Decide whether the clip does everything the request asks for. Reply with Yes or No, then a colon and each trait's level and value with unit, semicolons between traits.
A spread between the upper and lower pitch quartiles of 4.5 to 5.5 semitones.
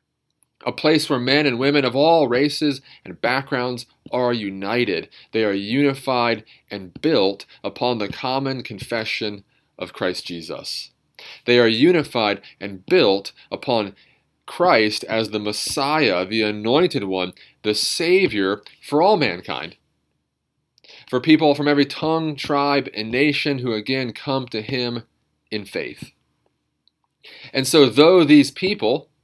Yes: average, 4.9 semitones